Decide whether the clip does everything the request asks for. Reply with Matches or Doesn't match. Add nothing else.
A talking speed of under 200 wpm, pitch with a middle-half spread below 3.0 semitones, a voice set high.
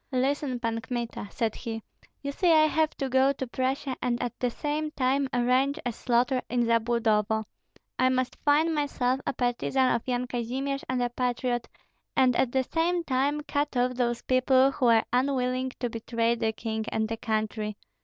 Matches